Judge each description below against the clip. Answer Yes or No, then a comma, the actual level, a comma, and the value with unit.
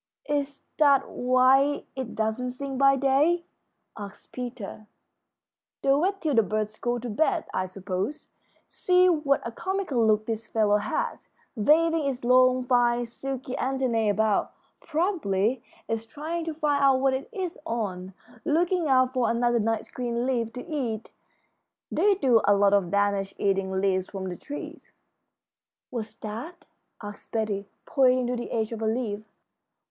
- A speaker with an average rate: Yes, average, 150 wpm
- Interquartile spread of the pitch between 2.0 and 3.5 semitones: No, average, 4.7 semitones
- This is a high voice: Yes, high, 245 Hz